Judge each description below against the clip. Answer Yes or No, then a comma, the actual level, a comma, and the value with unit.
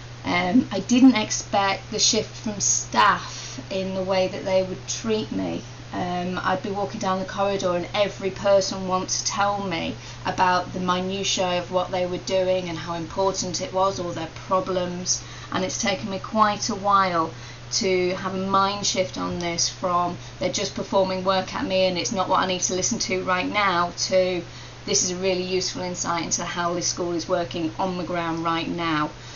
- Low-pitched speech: No, medium, 185 Hz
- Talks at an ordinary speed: Yes, average, 195 wpm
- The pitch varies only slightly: Yes, narrow, 1.9 semitones